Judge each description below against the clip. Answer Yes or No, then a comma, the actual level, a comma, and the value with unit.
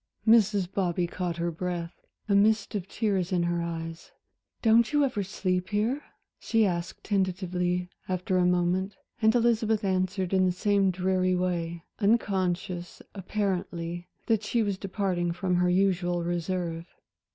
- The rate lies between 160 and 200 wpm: No, average, 140 wpm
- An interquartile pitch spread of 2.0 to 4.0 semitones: Yes, narrow, 2.6 semitones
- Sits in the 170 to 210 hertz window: Yes, medium, 185 Hz